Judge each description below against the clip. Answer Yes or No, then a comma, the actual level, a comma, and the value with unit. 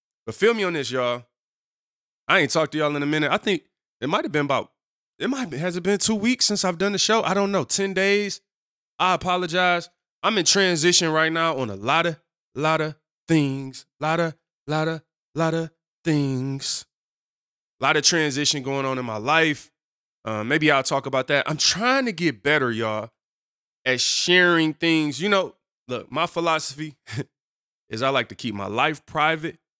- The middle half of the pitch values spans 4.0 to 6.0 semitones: Yes, average, 4.5 semitones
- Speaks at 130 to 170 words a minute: No, average, 190 wpm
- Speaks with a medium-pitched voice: Yes, medium, 160 Hz